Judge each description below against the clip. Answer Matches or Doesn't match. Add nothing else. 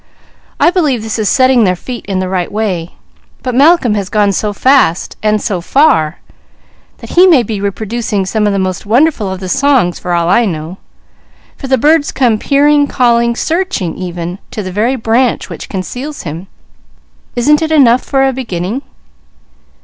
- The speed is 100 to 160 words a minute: Doesn't match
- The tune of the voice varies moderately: Doesn't match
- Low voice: Doesn't match